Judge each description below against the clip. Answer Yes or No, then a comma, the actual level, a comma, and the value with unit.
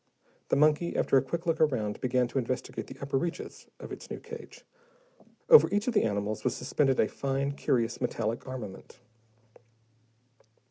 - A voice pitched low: Yes, low, 130 Hz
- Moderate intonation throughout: Yes, average, 4.5 semitones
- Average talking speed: Yes, average, 160 wpm